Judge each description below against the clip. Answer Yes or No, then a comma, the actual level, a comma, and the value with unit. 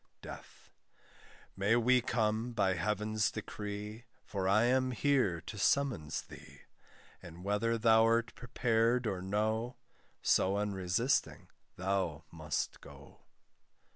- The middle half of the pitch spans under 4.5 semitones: Yes, average, 3.3 semitones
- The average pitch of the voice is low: Yes, low, 110 Hz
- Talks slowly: Yes, slow, 105 wpm